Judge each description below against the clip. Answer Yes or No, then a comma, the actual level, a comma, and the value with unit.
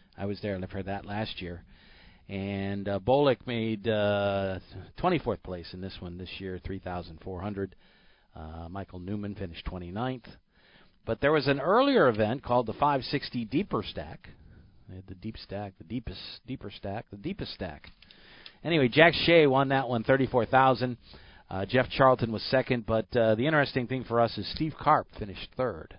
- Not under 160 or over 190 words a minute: Yes, average, 165 wpm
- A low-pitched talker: Yes, low, 105 Hz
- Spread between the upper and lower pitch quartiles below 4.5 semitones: No, average, 5.2 semitones